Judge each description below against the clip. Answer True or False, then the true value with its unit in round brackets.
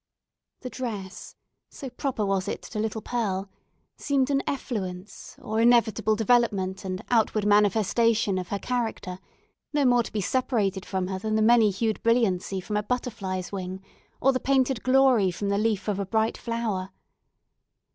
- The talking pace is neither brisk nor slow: True (160 wpm)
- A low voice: False (215 Hz)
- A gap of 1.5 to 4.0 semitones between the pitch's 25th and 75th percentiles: True (3.7 semitones)